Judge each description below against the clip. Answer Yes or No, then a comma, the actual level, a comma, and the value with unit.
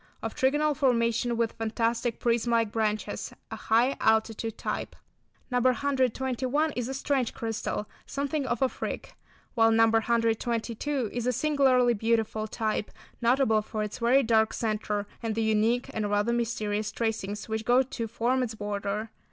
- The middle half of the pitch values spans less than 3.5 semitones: Yes, narrow, 2.4 semitones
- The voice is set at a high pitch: Yes, high, 230 Hz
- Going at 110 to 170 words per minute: Yes, average, 150 wpm